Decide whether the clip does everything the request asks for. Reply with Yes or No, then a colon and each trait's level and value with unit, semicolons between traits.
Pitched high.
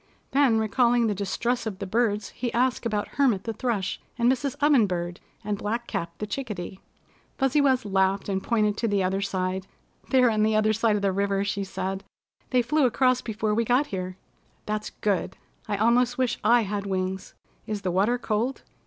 Yes: high, 215 Hz